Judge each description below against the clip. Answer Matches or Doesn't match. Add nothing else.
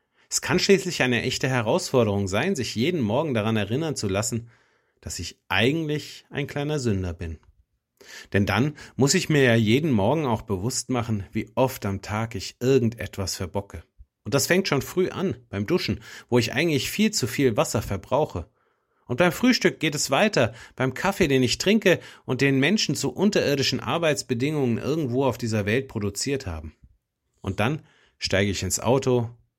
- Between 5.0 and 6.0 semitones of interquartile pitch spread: Matches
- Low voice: Matches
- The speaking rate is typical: Matches